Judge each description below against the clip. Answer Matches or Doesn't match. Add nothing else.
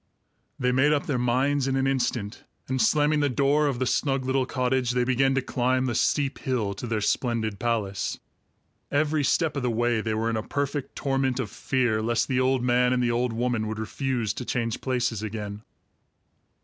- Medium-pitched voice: Doesn't match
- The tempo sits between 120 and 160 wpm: Doesn't match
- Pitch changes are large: Doesn't match